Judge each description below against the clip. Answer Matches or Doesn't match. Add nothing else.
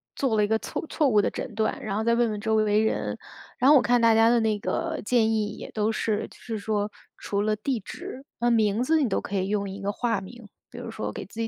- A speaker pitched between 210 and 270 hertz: Matches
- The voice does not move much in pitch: Matches